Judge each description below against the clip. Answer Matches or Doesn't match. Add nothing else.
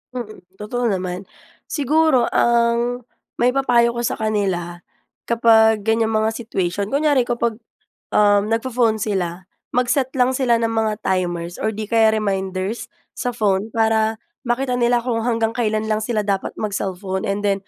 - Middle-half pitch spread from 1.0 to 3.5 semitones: Matches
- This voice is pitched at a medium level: Doesn't match